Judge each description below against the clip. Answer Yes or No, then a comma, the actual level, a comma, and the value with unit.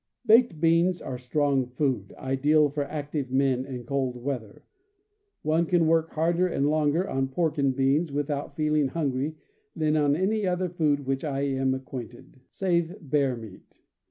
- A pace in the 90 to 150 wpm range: No, average, 160 wpm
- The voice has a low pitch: No, medium, 145 Hz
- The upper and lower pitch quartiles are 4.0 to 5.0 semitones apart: No, average, 3.4 semitones